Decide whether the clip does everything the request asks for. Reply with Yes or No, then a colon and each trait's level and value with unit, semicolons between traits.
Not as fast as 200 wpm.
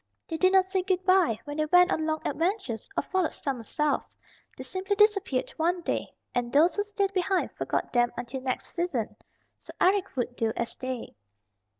Yes: average, 190 wpm